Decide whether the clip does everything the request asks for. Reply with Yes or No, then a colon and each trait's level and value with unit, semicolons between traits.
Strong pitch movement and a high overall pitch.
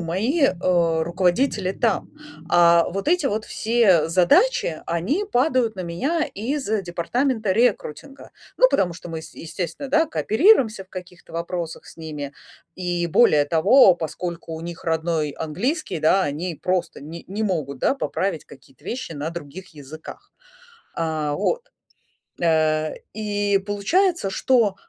No: wide, 6.2 semitones; medium, 180 Hz